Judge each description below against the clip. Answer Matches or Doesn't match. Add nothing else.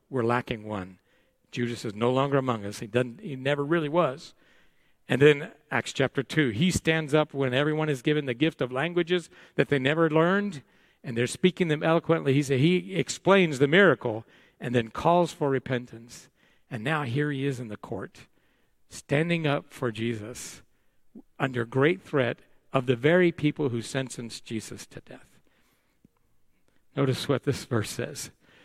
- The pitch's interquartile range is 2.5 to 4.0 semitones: Doesn't match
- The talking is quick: Doesn't match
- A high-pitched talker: Doesn't match